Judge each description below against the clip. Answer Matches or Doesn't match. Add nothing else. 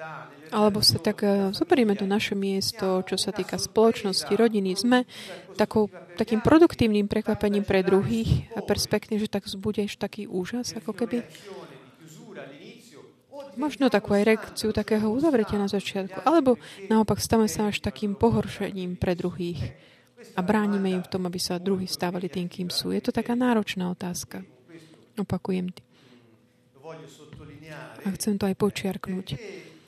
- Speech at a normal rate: Matches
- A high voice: Matches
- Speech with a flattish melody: Doesn't match